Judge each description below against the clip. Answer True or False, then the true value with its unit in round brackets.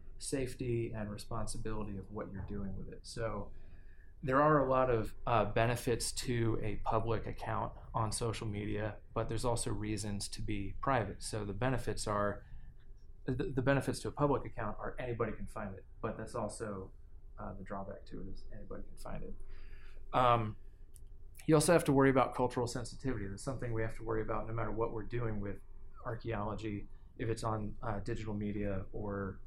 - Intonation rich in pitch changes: False (2.9 semitones)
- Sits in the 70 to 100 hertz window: False (110 Hz)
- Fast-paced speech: False (180 wpm)